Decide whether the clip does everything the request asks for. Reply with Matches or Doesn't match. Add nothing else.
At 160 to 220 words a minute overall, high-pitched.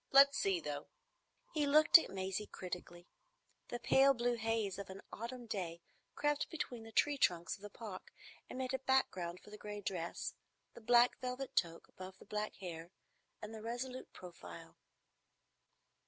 Matches